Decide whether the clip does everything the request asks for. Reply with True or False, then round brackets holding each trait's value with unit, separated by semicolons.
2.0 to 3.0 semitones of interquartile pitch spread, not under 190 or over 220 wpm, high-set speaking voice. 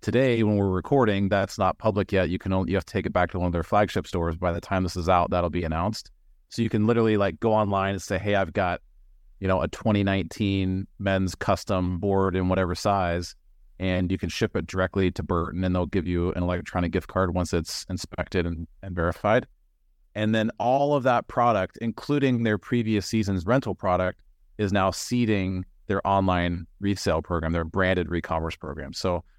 False (2.5 semitones; 205 wpm; 95 Hz)